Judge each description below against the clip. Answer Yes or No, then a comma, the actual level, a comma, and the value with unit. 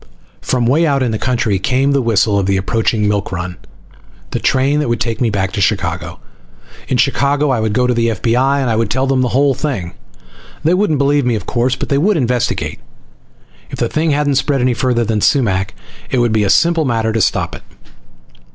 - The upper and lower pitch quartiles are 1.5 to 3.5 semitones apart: No, average, 4.1 semitones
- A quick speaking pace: Yes, fast, 210 wpm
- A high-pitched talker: No, low, 125 Hz